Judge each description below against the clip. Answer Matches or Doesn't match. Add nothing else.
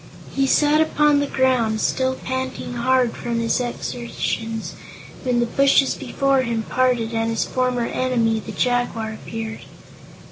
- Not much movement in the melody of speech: Matches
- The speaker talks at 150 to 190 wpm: Doesn't match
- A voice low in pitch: Doesn't match